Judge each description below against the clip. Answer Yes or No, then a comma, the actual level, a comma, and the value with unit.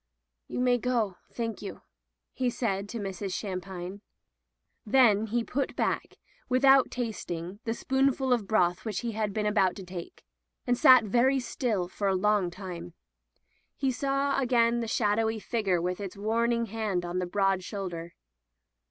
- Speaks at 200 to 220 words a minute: No, average, 160 wpm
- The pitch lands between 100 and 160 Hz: No, high, 215 Hz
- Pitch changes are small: No, average, 4.1 semitones